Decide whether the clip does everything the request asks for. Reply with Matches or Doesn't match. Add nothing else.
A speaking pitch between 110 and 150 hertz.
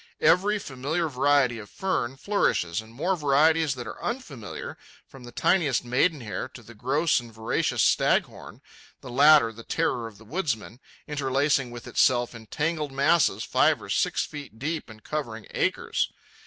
Matches